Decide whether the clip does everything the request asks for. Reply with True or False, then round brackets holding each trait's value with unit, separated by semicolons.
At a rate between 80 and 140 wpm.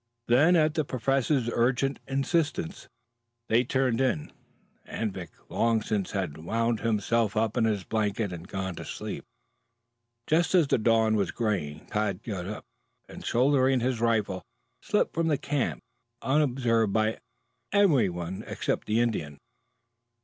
True (135 wpm)